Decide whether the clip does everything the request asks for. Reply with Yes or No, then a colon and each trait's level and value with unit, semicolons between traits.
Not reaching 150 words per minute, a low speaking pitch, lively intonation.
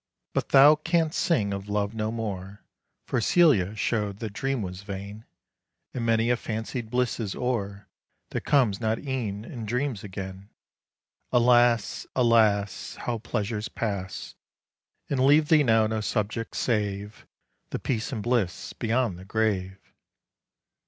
No: average, 140 wpm; low, 110 Hz; average, 3.3 semitones